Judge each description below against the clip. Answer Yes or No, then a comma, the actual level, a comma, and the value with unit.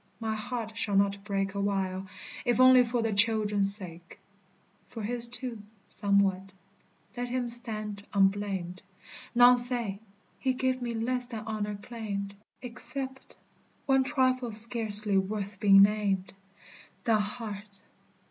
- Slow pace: Yes, slow, 125 wpm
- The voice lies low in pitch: No, high, 215 Hz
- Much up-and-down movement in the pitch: No, average, 3.4 semitones